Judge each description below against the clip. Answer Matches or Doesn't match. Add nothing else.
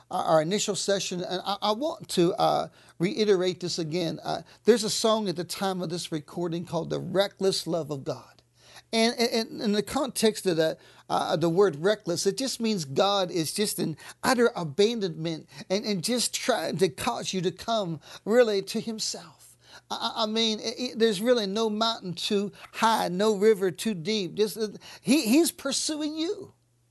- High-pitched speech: Matches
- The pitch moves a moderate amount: Matches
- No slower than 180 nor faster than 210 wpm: Matches